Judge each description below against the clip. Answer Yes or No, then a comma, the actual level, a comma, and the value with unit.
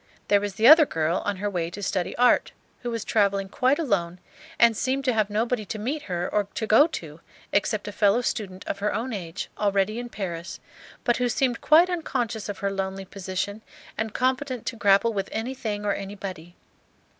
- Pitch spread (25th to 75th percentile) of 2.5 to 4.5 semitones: Yes, average, 3.6 semitones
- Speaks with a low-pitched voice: No, high, 210 Hz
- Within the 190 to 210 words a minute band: Yes, average, 195 wpm